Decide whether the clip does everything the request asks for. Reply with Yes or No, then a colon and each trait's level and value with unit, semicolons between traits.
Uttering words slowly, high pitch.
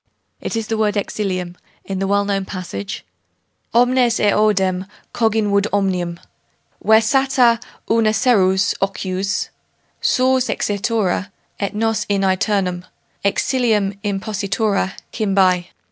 Yes: slow, 100 wpm; high, 200 Hz